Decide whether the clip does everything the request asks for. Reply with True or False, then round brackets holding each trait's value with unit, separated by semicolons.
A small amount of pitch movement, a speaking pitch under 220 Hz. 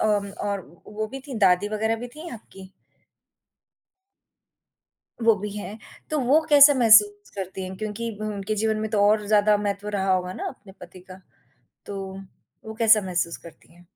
True (2.3 semitones; 210 Hz)